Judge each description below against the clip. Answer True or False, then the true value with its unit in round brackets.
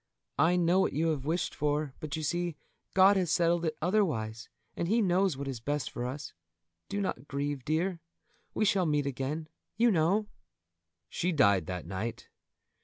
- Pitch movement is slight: False (4.6 semitones)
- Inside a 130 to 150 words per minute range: False (175 wpm)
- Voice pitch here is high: False (155 Hz)